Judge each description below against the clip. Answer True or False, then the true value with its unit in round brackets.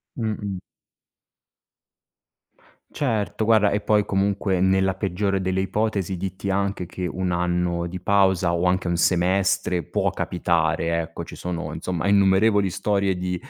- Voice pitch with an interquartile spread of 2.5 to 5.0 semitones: False (2.1 semitones)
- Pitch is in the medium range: False (95 Hz)